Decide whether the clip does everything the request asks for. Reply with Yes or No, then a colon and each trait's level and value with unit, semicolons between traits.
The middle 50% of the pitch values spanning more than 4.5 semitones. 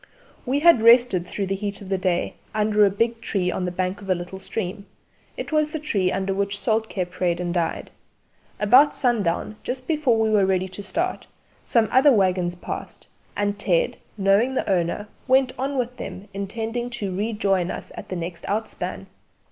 No: average, 4.1 semitones